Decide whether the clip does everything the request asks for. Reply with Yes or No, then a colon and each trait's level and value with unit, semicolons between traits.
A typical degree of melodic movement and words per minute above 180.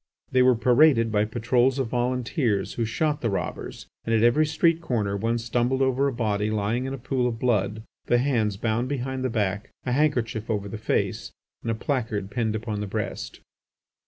Yes: average, 3.0 semitones; average, 190 wpm